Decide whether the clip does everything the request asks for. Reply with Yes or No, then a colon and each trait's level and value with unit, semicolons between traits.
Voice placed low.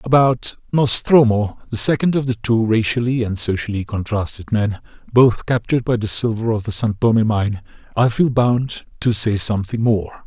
Yes: low, 115 Hz